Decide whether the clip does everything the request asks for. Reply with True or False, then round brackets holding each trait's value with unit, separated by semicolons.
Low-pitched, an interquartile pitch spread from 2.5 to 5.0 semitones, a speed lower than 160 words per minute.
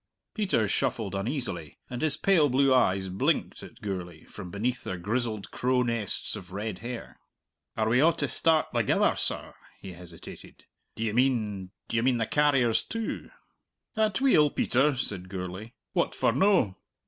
False (115 Hz; 5.6 semitones; 150 wpm)